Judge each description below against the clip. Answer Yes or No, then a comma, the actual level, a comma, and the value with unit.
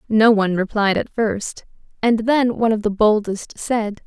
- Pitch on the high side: Yes, high, 215 Hz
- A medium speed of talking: Yes, average, 175 wpm